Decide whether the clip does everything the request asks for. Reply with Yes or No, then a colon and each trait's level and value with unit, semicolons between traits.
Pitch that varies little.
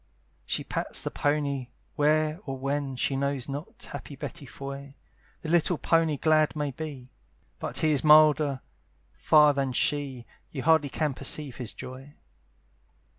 Yes: narrow, 2.2 semitones